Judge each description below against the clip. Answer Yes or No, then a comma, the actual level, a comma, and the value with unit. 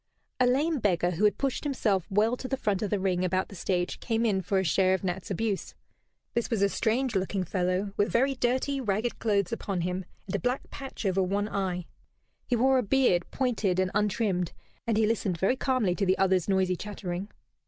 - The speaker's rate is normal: No, fast, 210 wpm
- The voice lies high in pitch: Yes, high, 200 Hz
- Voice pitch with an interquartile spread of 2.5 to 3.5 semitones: No, average, 4.0 semitones